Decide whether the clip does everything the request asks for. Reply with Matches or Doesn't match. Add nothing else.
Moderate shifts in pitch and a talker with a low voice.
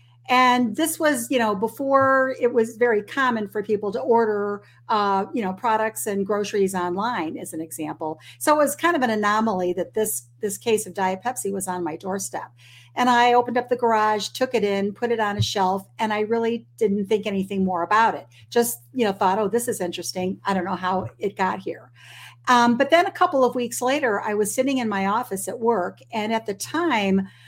Doesn't match